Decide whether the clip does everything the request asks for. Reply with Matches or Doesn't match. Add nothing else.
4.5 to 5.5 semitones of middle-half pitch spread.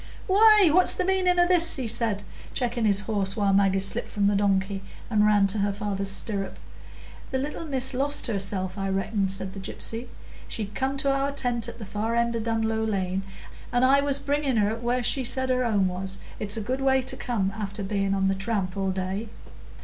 Matches